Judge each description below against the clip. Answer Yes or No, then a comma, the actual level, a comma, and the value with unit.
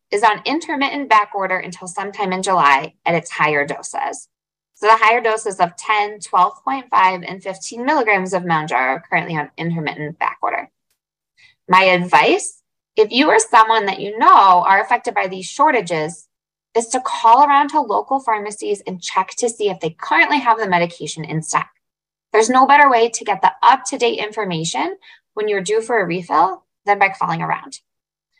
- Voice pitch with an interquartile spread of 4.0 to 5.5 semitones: Yes, average, 4.9 semitones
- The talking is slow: No, average, 175 wpm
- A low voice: No, high, 205 Hz